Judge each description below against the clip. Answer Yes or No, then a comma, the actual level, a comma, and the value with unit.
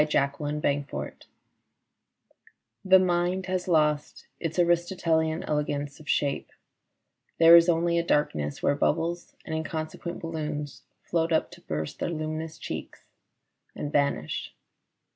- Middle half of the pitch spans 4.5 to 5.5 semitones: No, narrow, 2.5 semitones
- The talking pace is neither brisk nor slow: No, slow, 125 wpm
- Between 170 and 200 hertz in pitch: No, medium, 160 Hz